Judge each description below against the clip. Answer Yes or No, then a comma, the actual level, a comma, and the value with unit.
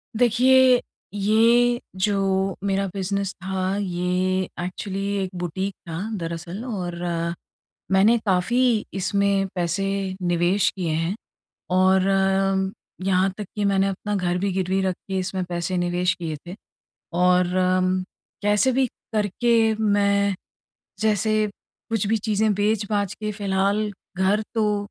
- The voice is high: Yes, high, 195 Hz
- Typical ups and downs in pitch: No, narrow, 2.3 semitones